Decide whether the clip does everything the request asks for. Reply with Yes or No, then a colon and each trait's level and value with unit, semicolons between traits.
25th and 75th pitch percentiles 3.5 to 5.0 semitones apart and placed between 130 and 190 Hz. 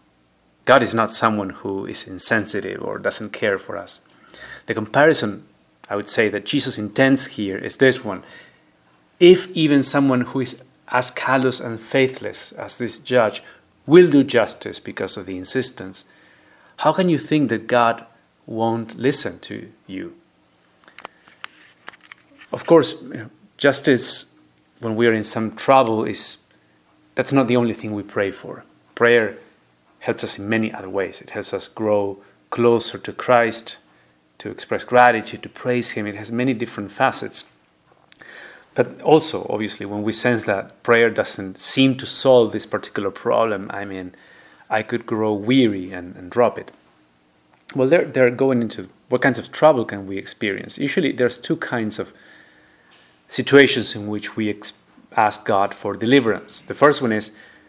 No: average, 4.2 semitones; low, 115 Hz